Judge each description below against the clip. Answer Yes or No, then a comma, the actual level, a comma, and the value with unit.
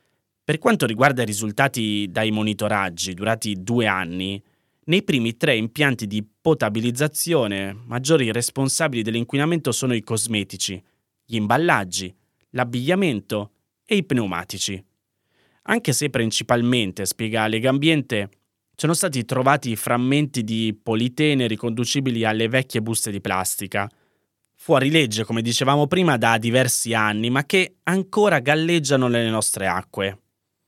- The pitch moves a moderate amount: Yes, average, 4.5 semitones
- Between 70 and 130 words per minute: Yes, average, 120 wpm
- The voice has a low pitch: Yes, low, 115 Hz